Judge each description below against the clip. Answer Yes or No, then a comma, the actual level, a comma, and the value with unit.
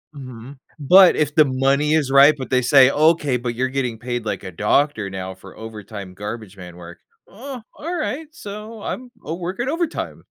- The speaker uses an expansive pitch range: Yes, wide, 7.6 semitones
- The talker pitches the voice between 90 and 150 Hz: Yes, low, 135 Hz